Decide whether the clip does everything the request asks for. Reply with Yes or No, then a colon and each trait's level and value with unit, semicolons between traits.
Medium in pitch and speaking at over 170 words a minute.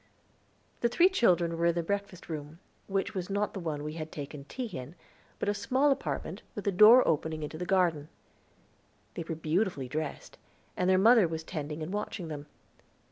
Yes: medium, 170 Hz; average, 190 wpm